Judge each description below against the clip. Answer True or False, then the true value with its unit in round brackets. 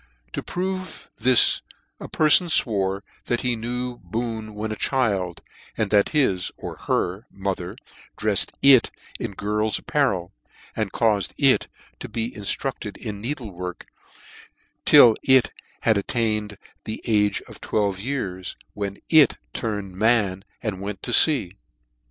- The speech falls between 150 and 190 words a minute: False (135 wpm)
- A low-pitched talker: True (110 Hz)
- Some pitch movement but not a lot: True (3.7 semitones)